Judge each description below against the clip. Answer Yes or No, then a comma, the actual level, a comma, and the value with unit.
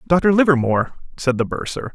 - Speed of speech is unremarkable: Yes, average, 155 wpm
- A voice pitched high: No, medium, 150 Hz